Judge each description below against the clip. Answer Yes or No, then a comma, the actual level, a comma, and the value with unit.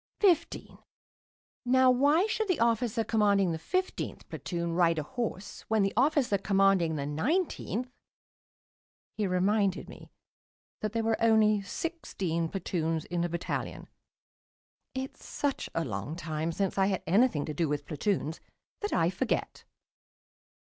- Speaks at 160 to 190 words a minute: No, average, 140 wpm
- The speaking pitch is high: Yes, high, 200 Hz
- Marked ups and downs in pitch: Yes, wide, 6.5 semitones